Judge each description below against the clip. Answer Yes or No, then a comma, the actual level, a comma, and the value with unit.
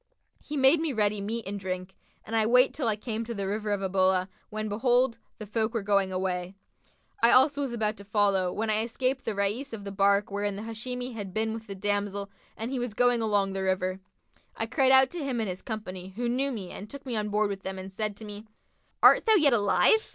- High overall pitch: Yes, high, 215 Hz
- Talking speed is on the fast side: Yes, fast, 240 wpm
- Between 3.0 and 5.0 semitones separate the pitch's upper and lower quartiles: Yes, average, 3.3 semitones